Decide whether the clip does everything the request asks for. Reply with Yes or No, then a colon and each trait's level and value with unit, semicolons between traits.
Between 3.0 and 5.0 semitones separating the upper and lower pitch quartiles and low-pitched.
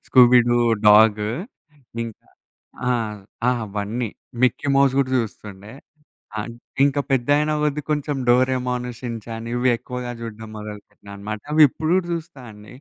Yes: average, 3.8 semitones; low, 120 Hz